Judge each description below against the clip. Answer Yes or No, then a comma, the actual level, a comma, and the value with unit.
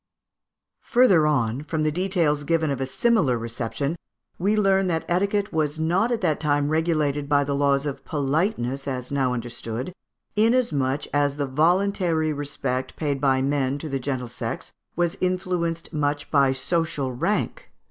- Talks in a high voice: No, medium, 150 Hz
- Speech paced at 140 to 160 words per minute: Yes, average, 155 wpm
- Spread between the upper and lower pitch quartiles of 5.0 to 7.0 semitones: No, average, 4.1 semitones